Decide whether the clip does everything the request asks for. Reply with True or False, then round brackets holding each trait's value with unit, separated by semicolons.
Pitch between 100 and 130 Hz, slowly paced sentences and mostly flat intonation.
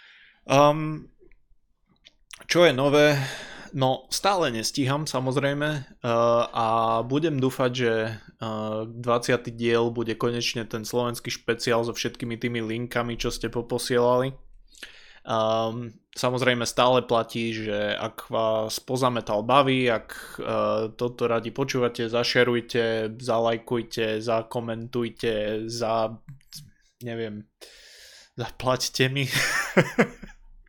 True (120 Hz; 95 wpm; 2.2 semitones)